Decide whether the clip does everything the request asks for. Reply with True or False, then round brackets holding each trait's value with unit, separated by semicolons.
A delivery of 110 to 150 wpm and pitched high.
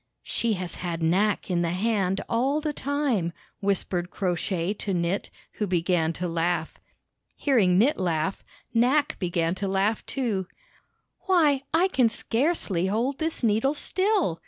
True (145 wpm; 200 Hz)